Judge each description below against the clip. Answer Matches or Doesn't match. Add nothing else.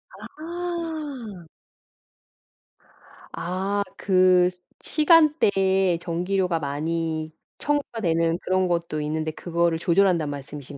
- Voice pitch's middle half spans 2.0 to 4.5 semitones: Matches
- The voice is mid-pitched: Matches